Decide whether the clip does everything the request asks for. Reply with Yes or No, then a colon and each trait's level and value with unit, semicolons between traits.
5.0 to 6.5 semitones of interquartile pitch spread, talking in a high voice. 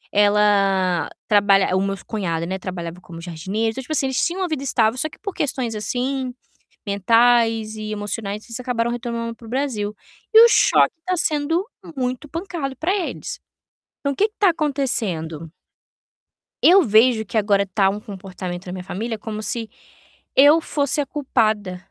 Yes: wide, 5.6 semitones; high, 225 Hz